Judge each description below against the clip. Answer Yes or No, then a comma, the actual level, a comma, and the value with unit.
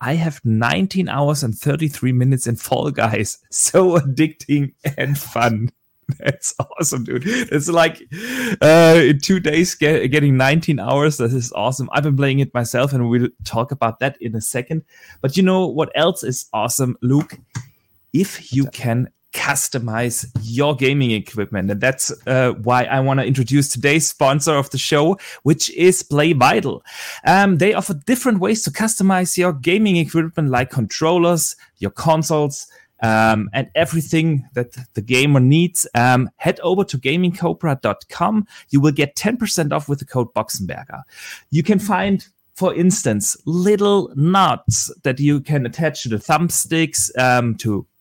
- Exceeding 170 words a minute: No, average, 155 wpm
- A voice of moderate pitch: Yes, medium, 145 Hz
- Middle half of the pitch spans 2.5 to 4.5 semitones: No, average, 5.0 semitones